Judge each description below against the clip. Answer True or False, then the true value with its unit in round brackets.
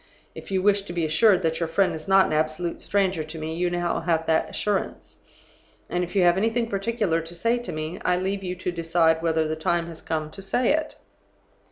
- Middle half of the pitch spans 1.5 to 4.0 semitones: True (3.2 semitones)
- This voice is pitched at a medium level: True (175 Hz)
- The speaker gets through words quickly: True (225 wpm)